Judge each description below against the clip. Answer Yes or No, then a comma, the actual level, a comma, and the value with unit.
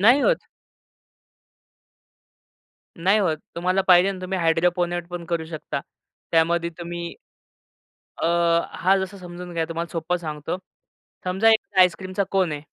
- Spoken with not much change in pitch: Yes, narrow, 1.9 semitones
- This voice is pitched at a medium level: Yes, medium, 175 Hz